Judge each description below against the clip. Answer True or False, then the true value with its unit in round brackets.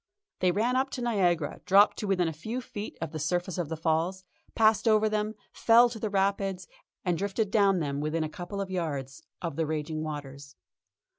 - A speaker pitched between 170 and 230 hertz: True (185 Hz)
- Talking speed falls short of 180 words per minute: False (200 wpm)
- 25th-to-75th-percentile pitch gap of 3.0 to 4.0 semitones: False (4.9 semitones)